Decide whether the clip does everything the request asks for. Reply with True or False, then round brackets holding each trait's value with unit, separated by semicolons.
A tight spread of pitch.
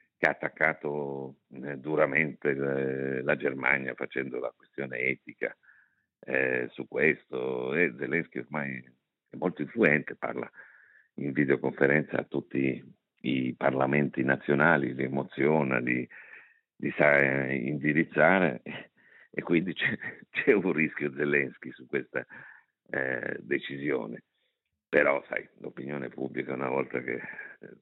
True (1.6 semitones)